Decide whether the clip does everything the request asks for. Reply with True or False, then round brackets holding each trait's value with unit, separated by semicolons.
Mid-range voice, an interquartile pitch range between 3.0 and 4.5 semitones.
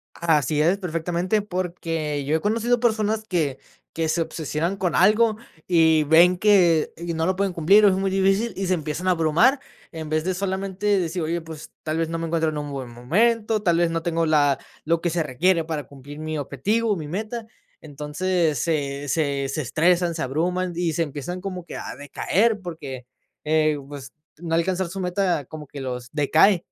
True (165 Hz; 3.5 semitones)